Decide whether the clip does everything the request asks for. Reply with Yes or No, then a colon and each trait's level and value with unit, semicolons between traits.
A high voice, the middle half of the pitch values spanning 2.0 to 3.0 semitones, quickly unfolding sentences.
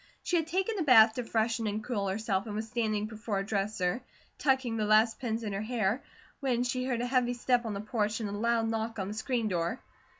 Yes: high, 225 Hz; average, 2.7 semitones; fast, 235 wpm